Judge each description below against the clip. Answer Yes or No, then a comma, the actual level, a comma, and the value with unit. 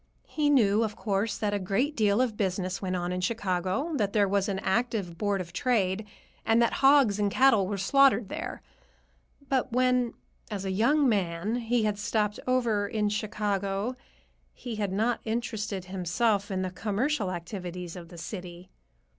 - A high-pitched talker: Yes, high, 205 Hz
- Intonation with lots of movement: No, average, 3.5 semitones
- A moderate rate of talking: Yes, average, 170 wpm